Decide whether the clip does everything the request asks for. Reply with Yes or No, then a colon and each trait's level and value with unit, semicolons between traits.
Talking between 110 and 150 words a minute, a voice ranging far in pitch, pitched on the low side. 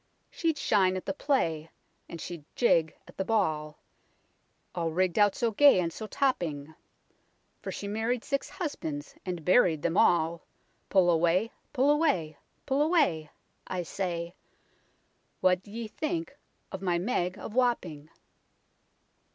No: average, 140 wpm; wide, 6.6 semitones; medium, 185 Hz